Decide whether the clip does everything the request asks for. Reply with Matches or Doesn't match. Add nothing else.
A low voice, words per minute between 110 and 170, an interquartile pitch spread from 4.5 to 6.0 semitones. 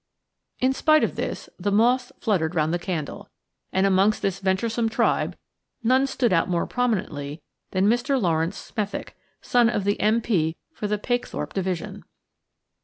Doesn't match